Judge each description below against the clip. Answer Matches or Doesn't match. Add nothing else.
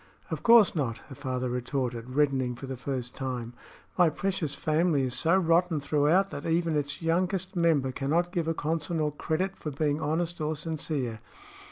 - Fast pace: Doesn't match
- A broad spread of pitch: Doesn't match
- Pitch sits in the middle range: Matches